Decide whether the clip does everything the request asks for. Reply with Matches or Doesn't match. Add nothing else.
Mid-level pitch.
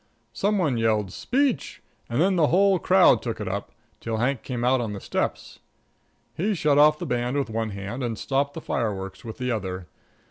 Doesn't match